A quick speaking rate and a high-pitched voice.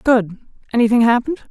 No: slow, 120 wpm; high, 240 Hz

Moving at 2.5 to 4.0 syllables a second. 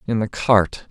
Yes: 3.9 syllables/s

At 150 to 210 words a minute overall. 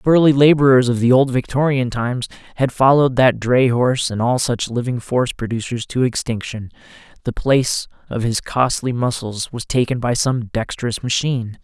Yes: average, 170 wpm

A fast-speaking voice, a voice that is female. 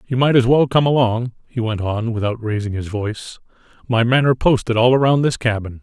No: fast, 215 wpm; male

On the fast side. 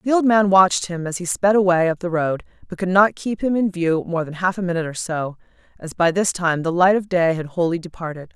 Yes: fast, 265 wpm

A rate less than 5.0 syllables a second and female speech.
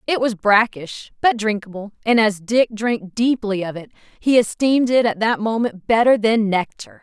Yes: 4.7 syllables/s; female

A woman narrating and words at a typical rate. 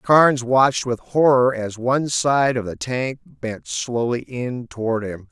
No: male; average, 170 wpm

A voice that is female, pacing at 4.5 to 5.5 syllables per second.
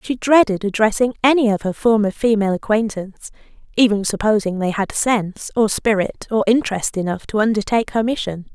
No: female; 5.8 syllables/s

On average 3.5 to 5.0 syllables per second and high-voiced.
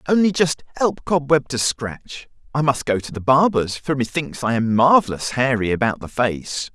No: 4.7 syllables/s; low, 135 Hz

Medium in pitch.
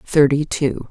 Yes: medium, 145 Hz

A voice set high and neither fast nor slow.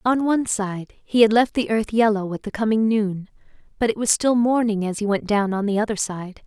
No: high, 215 Hz; fast, 240 wpm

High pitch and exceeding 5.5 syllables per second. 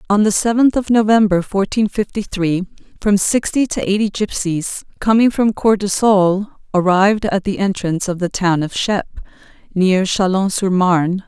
No: high, 195 Hz; 5.0 syllables/s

